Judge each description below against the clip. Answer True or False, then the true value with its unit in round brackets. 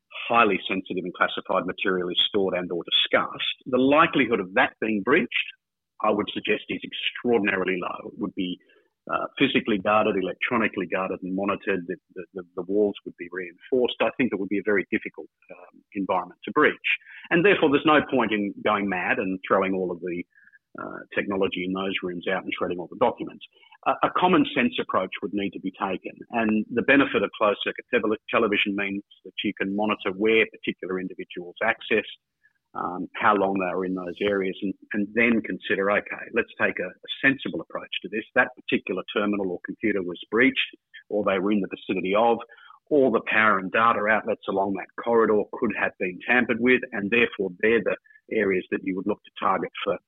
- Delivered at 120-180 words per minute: False (195 wpm)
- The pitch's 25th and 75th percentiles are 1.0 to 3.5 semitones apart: True (2.9 semitones)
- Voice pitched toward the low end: True (100 Hz)